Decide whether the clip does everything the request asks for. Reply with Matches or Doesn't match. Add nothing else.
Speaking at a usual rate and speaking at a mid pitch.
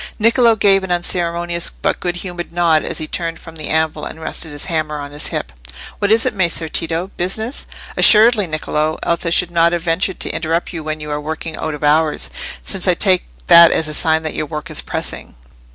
Doesn't match